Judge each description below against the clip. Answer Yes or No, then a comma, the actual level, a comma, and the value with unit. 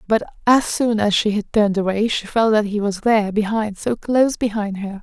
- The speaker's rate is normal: No, fast, 225 wpm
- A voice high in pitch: Yes, high, 210 Hz